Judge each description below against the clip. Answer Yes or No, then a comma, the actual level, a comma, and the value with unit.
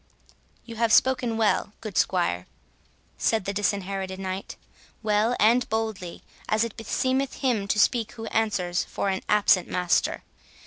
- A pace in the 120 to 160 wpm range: Yes, average, 140 wpm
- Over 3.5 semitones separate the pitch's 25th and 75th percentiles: No, average, 2.9 semitones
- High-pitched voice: Yes, high, 210 Hz